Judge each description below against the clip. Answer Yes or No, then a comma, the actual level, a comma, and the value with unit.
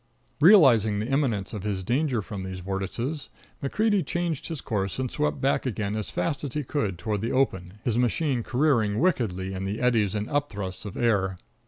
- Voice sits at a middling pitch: No, low, 115 Hz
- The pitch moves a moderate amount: No, wide, 6.0 semitones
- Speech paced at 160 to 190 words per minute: Yes, average, 185 wpm